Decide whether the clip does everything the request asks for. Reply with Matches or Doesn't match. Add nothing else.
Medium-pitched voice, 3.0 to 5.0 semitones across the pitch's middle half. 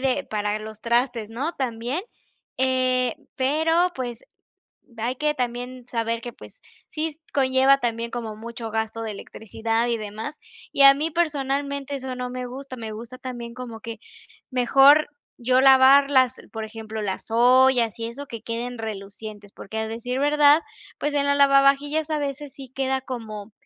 Doesn't match